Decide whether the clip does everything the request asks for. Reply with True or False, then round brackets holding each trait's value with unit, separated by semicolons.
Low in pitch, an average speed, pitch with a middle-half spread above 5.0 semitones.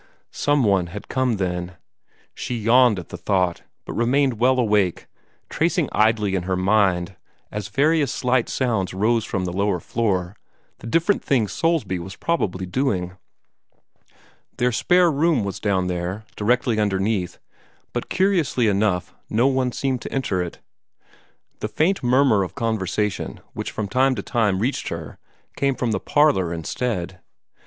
True (110 Hz; 145 wpm; 5.5 semitones)